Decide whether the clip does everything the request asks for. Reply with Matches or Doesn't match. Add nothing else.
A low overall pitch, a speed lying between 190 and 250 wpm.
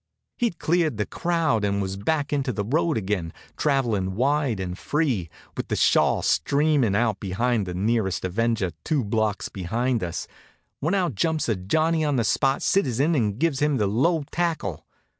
Doesn't match